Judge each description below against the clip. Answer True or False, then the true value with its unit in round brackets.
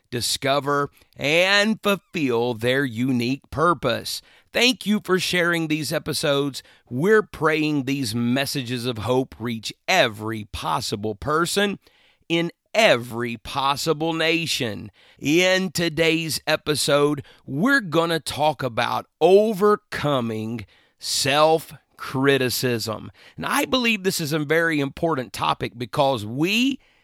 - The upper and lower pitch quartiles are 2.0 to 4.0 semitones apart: False (5.1 semitones)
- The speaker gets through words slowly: True (105 wpm)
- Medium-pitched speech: True (150 Hz)